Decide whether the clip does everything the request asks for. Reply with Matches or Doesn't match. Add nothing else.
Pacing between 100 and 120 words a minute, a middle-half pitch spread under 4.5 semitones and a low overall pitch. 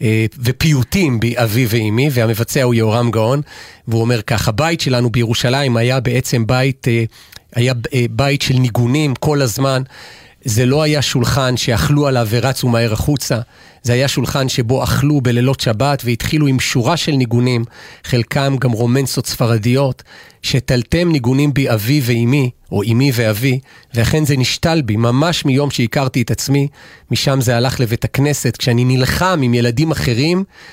Doesn't match